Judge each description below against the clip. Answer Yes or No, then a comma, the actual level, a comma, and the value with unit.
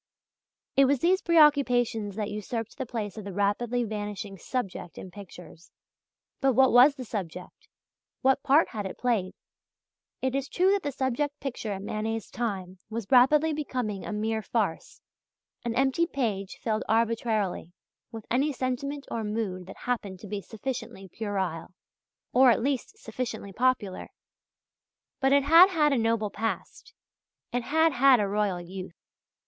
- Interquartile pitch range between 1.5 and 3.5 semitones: No, average, 4.7 semitones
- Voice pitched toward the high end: Yes, high, 230 Hz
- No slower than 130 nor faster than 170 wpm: Yes, average, 155 wpm